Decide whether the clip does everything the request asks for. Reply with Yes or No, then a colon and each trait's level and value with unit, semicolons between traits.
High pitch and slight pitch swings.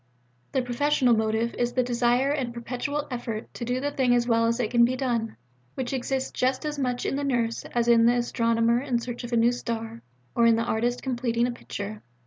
Yes: high, 240 Hz; narrow, 1.7 semitones